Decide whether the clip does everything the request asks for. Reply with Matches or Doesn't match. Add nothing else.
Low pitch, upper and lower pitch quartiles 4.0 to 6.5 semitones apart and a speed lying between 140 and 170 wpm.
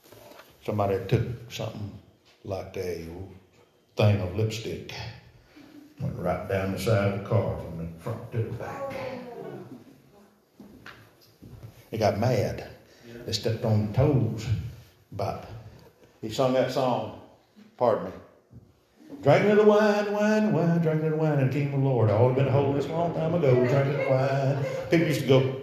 Matches